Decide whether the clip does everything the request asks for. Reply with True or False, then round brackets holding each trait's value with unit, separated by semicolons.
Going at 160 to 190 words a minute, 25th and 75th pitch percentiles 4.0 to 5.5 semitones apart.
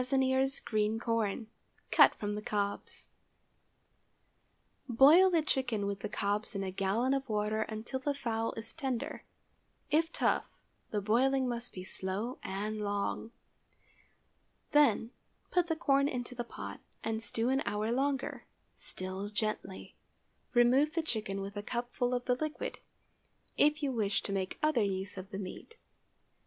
False (140 wpm; 4.5 semitones)